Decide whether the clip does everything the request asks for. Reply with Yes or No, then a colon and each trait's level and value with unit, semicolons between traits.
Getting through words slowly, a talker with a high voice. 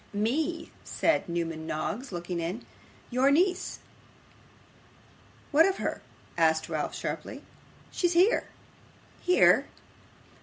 Yes: slow, 100 wpm; high, 230 Hz